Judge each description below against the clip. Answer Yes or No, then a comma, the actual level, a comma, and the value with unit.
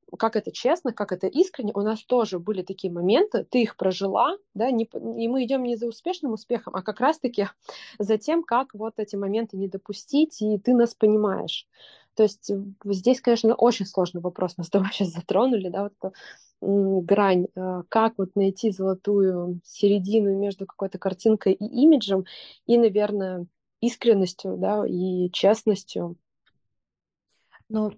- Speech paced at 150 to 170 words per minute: Yes, average, 155 wpm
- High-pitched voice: Yes, high, 210 Hz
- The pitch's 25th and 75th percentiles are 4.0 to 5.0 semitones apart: No, average, 3.2 semitones